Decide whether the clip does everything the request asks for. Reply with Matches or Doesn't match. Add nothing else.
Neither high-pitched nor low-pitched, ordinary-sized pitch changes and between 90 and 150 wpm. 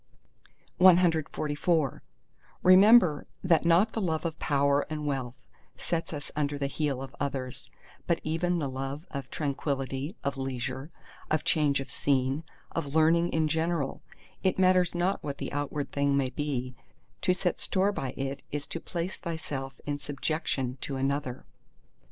Matches